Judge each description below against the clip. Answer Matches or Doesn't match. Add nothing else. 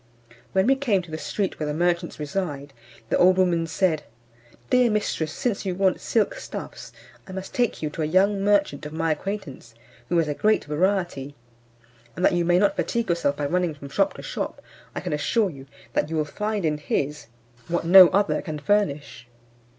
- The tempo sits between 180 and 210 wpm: Matches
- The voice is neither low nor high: Matches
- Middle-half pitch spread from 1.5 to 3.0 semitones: Doesn't match